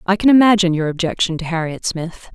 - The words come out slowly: No, fast, 205 wpm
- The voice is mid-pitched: Yes, medium, 180 Hz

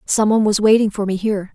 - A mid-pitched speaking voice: No, high, 205 Hz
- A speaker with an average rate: No, fast, 270 wpm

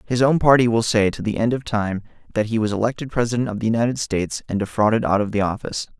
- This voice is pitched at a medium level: No, low, 110 Hz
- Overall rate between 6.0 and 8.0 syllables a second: Yes, 6.9 syllables/s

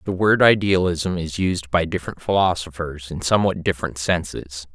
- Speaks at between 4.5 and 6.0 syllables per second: Yes, 5.2 syllables/s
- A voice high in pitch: No, very low, 85 Hz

